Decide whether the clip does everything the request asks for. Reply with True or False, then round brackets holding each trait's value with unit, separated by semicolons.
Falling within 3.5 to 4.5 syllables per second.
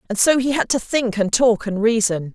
False (5.1 syllables/s)